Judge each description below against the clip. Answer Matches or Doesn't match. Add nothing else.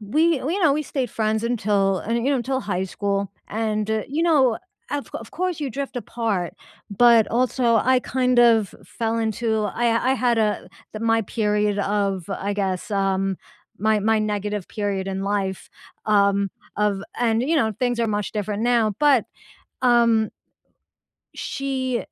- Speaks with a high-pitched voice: Matches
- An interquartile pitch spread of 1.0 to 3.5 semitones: Matches